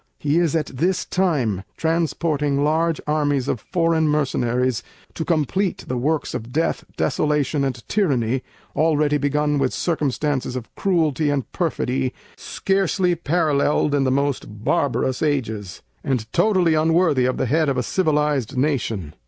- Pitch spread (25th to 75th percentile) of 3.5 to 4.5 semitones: Yes, average, 3.8 semitones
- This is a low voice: No, medium, 145 Hz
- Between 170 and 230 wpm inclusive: No, average, 140 wpm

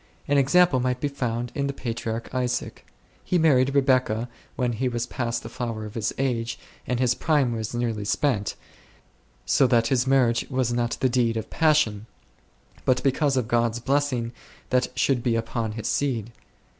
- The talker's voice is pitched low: Yes, low, 125 Hz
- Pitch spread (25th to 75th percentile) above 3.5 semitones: No, narrow, 2.5 semitones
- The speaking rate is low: No, average, 175 wpm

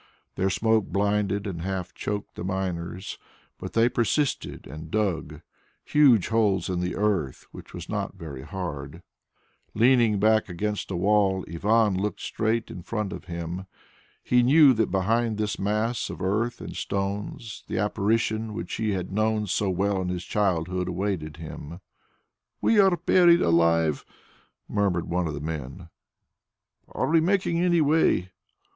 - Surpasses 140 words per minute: Yes, average, 150 wpm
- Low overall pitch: Yes, low, 100 Hz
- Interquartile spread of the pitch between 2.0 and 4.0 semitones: Yes, average, 3.7 semitones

